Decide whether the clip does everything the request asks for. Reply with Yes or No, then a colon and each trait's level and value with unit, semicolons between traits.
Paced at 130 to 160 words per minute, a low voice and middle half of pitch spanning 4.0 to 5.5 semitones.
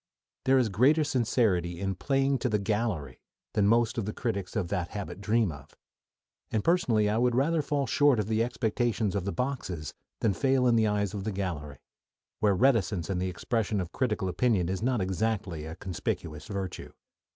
No: average, 190 wpm; low, 105 Hz; average, 4.5 semitones